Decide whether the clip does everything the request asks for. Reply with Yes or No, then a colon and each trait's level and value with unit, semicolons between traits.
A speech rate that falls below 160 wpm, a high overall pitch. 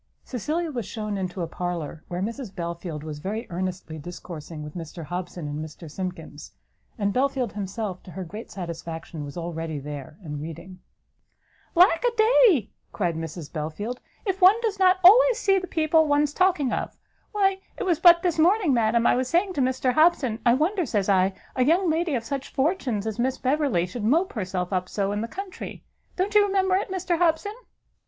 No: average, 190 wpm; high, 230 Hz